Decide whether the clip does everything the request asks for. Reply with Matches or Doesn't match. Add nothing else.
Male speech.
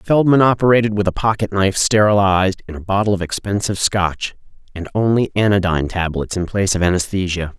Matches